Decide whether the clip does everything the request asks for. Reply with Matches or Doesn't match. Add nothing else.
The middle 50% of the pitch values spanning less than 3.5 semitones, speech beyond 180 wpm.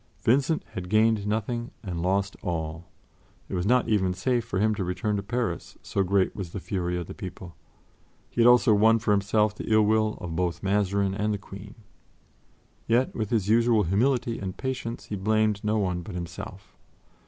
Matches